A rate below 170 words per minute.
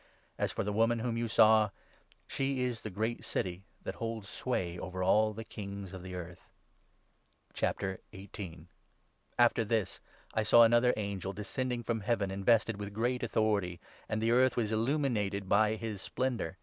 Yes: average, 160 wpm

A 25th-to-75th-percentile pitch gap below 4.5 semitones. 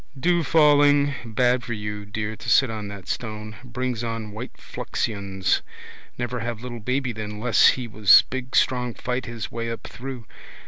Yes: average, 2.9 semitones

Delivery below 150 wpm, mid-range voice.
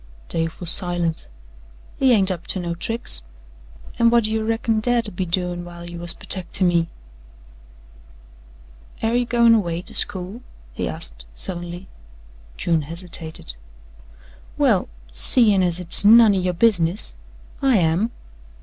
Yes: average, 140 wpm; medium, 180 Hz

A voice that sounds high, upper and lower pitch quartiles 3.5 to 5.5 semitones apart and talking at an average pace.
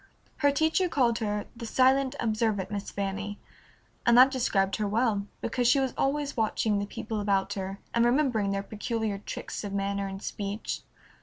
Yes: high, 215 Hz; average, 3.9 semitones; average, 170 wpm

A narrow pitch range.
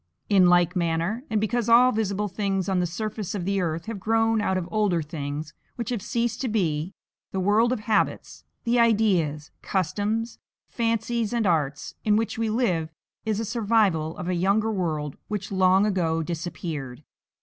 No: average, 4.5 semitones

